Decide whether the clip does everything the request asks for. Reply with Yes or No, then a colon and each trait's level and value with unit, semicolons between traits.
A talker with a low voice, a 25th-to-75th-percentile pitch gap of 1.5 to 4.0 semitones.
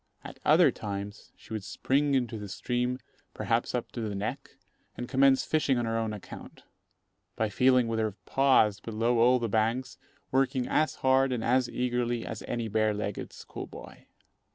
Yes: low, 120 Hz; average, 3.0 semitones